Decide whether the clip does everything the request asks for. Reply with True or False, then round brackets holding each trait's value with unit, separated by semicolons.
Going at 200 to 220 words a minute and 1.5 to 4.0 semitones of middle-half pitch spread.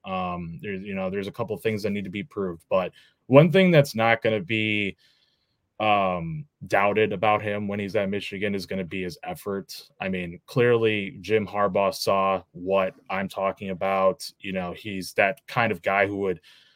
False (190 wpm; 3.0 semitones)